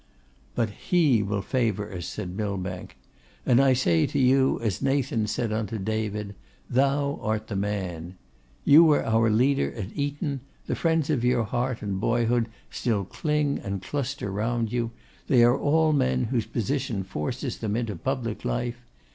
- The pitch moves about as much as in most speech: Yes, average, 4.6 semitones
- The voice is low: Yes, low, 115 Hz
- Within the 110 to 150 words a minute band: No, average, 160 wpm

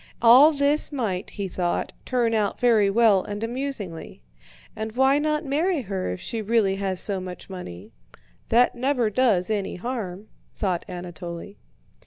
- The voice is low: No, high, 215 Hz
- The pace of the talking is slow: No, average, 150 wpm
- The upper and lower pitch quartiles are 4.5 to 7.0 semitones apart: Yes, average, 5.2 semitones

